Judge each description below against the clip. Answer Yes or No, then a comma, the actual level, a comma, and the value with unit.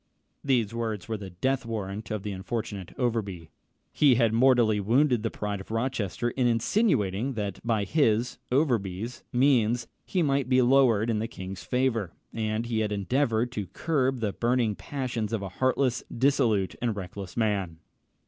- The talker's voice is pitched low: Yes, low, 115 Hz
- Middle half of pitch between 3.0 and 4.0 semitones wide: Yes, average, 3.7 semitones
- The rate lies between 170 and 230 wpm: No, average, 160 wpm